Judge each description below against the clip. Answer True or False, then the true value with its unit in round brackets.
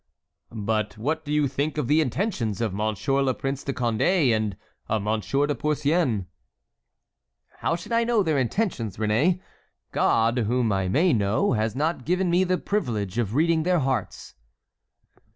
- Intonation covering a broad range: True (6.6 semitones)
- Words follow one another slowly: False (160 wpm)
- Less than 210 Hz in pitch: True (135 Hz)